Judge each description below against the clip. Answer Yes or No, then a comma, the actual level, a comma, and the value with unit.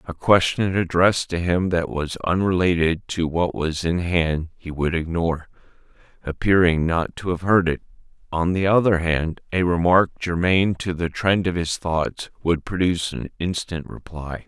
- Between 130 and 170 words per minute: Yes, average, 165 wpm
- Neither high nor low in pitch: No, very low, 85 Hz